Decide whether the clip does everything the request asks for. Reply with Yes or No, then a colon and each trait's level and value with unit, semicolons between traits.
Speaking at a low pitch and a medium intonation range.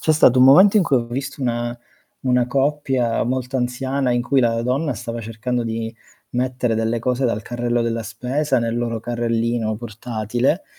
No: low, 120 Hz; narrow, 2.1 semitones